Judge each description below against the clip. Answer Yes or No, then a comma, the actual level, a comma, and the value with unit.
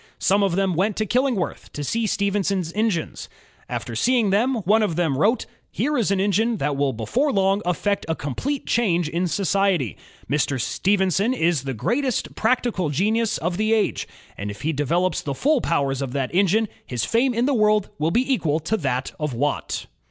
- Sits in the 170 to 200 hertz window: Yes, high, 190 Hz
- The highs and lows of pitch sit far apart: Yes, wide, 6.5 semitones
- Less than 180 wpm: No, average, 190 wpm